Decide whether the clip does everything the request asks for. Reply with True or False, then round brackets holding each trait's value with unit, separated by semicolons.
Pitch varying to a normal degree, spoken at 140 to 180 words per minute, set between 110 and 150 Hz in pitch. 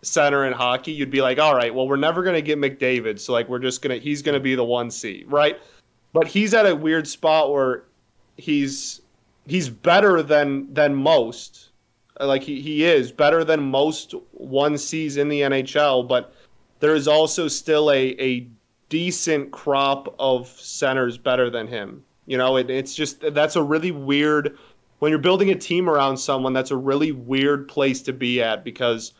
False (3.0 semitones; 190 wpm; 140 Hz)